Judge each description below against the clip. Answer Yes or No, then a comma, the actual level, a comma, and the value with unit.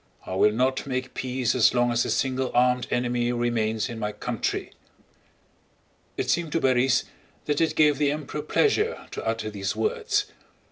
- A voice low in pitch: Yes, low, 125 Hz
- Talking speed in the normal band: Yes, average, 170 wpm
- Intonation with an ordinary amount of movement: Yes, average, 3.8 semitones